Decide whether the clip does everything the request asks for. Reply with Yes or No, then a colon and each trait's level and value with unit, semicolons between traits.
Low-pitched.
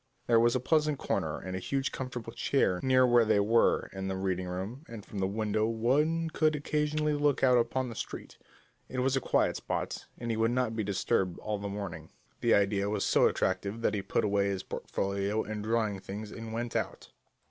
Yes: low, 110 Hz